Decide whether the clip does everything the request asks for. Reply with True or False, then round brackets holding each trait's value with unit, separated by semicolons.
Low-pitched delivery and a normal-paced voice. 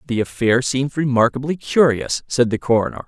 True (125 Hz; 155 wpm)